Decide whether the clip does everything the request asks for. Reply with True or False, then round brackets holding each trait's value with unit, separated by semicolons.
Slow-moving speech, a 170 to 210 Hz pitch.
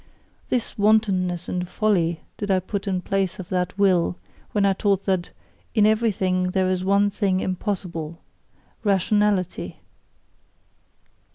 True (125 wpm; 190 Hz)